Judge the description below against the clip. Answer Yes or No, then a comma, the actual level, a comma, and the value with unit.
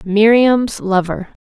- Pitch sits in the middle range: No, high, 210 Hz